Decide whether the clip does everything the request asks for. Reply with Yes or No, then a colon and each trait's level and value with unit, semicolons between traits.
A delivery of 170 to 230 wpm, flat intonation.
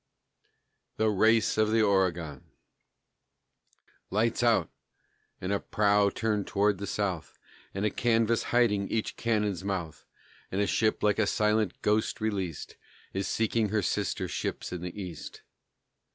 No: slow, 135 wpm; narrow, 2.2 semitones